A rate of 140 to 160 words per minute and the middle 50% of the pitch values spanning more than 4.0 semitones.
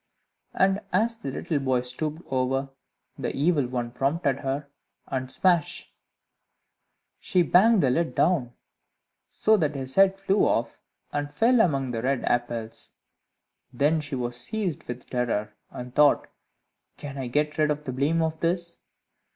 Yes: average, 150 wpm; average, 5.0 semitones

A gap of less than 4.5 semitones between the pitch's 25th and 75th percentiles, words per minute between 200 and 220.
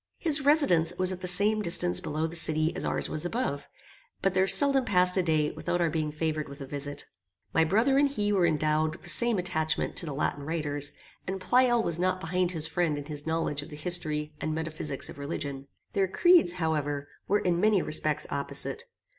Yes: average, 3.8 semitones; fast, 205 wpm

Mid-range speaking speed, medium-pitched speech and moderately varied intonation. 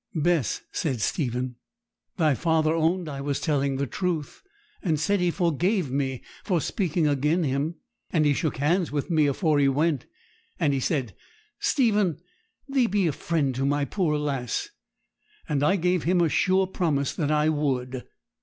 Yes: average, 165 wpm; medium, 155 Hz; average, 3.9 semitones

